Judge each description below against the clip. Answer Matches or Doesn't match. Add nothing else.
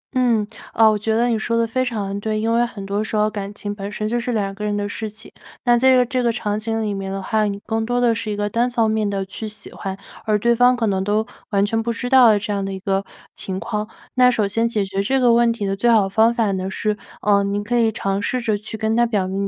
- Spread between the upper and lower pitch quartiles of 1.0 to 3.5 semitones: Matches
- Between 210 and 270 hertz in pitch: Matches